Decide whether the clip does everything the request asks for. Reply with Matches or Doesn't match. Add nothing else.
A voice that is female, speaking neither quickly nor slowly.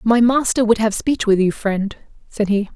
Doesn't match